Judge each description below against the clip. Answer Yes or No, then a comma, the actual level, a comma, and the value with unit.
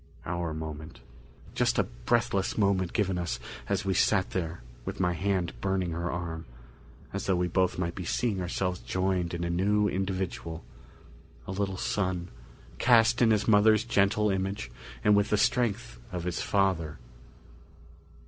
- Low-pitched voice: Yes, very low, 95 Hz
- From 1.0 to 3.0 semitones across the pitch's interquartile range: Yes, average, 2.7 semitones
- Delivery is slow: No, average, 155 wpm